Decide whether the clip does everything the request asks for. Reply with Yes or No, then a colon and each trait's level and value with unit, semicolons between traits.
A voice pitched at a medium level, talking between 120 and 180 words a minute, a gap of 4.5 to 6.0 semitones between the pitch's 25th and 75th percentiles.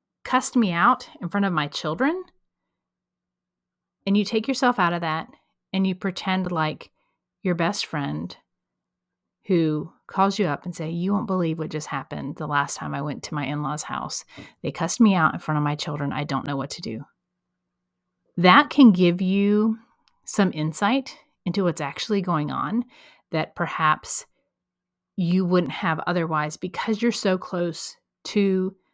Yes: medium, 175 Hz; average, 165 wpm; average, 5.3 semitones